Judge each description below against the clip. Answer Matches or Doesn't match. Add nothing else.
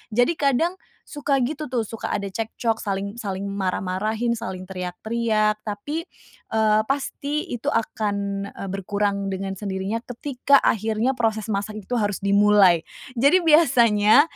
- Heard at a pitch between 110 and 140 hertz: Doesn't match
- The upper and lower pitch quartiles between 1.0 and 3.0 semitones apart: Doesn't match